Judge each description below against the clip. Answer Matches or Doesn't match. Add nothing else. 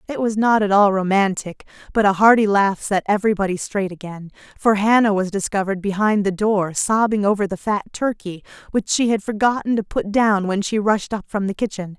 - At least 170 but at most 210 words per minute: Matches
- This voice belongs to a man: Doesn't match